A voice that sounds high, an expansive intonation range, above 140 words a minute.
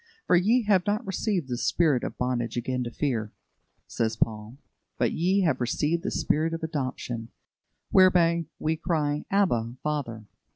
No: medium, 150 Hz; wide, 6.5 semitones; average, 155 wpm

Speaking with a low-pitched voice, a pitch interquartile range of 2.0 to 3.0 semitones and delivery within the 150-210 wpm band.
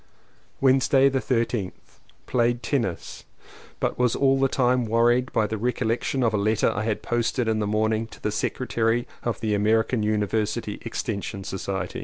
Yes: low, 115 Hz; narrow, 2.6 semitones; average, 170 wpm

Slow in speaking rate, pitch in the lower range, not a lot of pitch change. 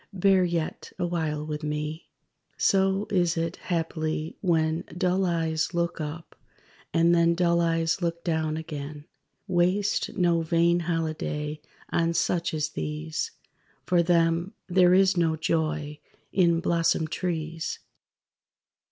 No: slow, 120 wpm; medium, 165 Hz; narrow, 1.8 semitones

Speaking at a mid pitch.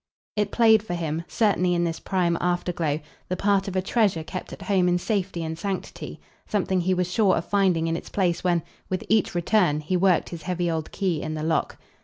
Yes: medium, 180 Hz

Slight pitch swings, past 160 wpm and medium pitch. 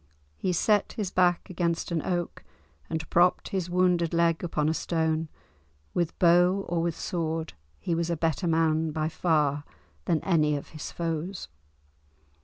No: narrow, 1.8 semitones; average, 155 wpm; medium, 170 Hz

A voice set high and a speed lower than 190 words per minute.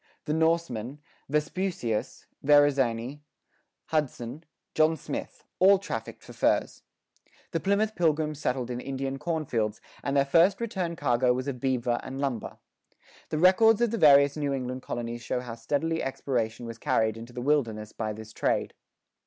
No: medium, 140 Hz; average, 150 wpm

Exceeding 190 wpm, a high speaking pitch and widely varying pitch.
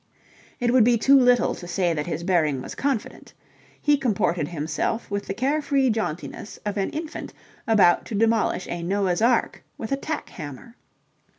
No: average, 175 wpm; high, 215 Hz; wide, 6.1 semitones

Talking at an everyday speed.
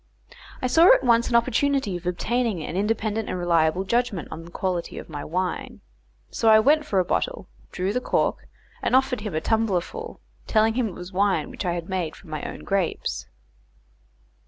Yes: average, 190 wpm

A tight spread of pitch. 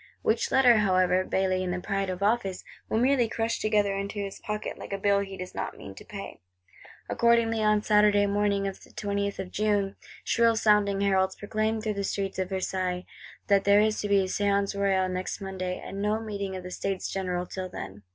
Yes: narrow, 1.9 semitones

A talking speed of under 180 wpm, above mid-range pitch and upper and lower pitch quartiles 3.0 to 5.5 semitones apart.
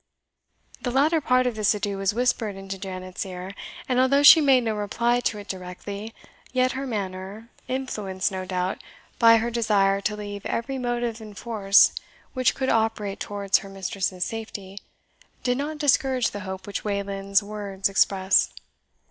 Yes: average, 160 wpm; high, 210 Hz; average, 3.8 semitones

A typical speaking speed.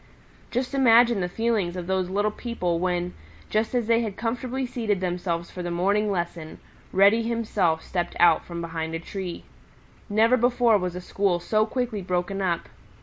Yes: average, 170 wpm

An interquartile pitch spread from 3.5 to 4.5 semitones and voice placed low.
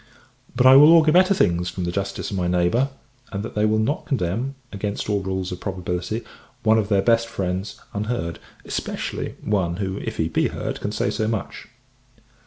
Yes: average, 4.0 semitones; low, 100 Hz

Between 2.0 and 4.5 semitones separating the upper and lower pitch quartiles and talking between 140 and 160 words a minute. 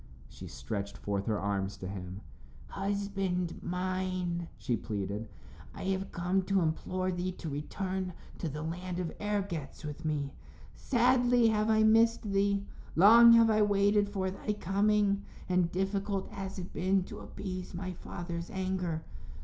Yes: average, 3.5 semitones; average, 150 wpm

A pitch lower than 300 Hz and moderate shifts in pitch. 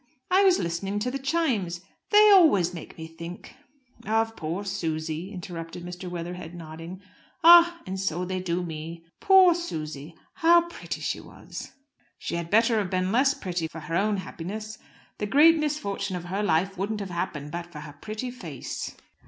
No: medium, 185 Hz; wide, 5.9 semitones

